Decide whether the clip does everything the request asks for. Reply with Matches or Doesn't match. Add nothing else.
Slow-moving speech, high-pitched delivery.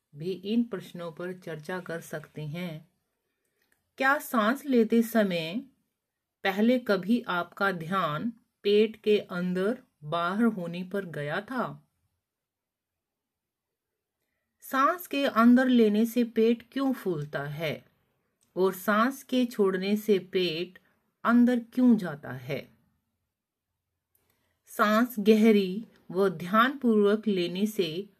Matches